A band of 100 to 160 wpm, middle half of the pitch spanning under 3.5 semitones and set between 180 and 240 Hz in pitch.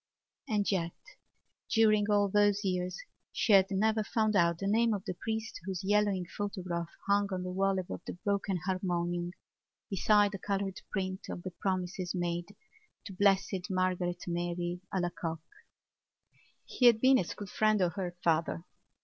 Yes: average, 155 wpm; narrow, 2.6 semitones; high, 190 Hz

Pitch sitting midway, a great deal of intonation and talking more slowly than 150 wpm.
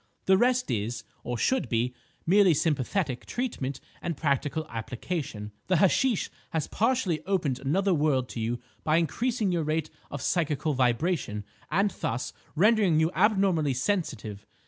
Yes: medium, 155 Hz; wide, 6.9 semitones; average, 140 wpm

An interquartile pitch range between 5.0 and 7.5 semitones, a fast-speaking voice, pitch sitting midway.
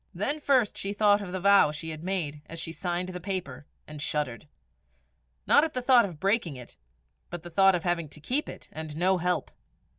No: average, 4.1 semitones; fast, 215 wpm; medium, 180 Hz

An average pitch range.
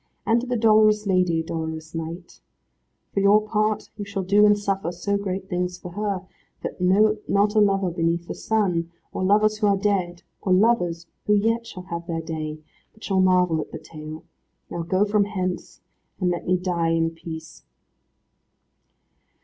Yes: average, 3.5 semitones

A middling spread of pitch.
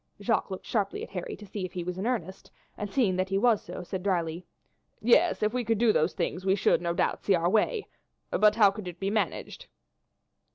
Yes: average, 3.3 semitones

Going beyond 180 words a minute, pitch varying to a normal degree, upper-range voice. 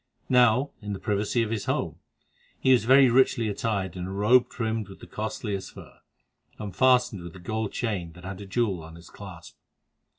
No: average, 195 wpm; average, 3.9 semitones; low, 105 Hz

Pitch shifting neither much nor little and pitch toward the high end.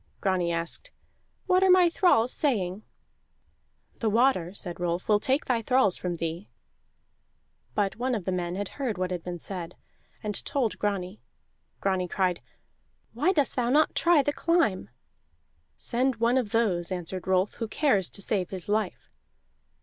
No: wide, 6.0 semitones; high, 205 Hz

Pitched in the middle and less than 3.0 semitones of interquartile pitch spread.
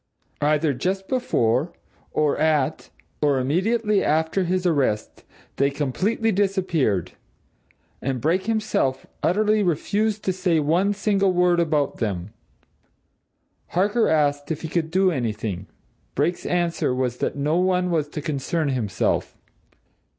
No: medium, 160 Hz; average, 5.1 semitones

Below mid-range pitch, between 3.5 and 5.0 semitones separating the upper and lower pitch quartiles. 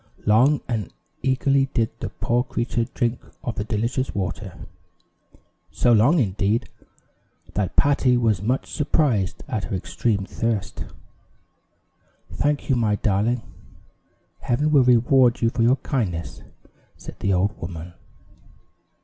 Yes: low, 115 Hz; average, 3.9 semitones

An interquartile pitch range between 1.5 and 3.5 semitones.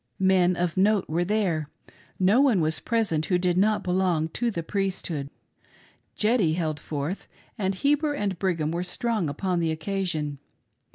No: average, 4.2 semitones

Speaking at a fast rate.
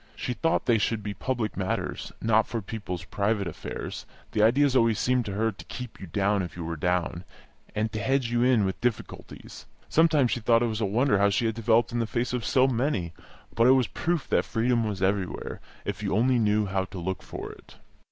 Yes: fast, 230 wpm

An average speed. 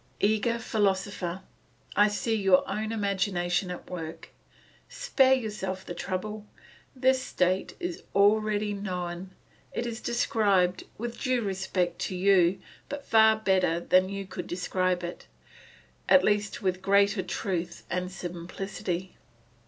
No: slow, 120 wpm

